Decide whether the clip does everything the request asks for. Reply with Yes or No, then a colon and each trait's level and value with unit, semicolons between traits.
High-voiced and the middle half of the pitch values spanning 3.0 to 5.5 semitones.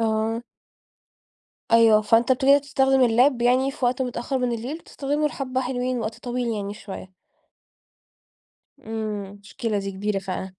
Yes: high, 235 Hz; average, 3.4 semitones